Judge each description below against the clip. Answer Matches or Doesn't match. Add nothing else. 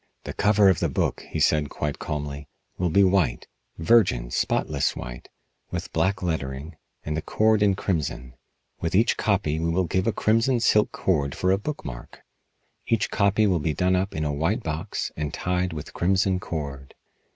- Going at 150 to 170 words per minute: Doesn't match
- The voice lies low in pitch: Matches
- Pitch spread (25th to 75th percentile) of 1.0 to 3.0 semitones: Doesn't match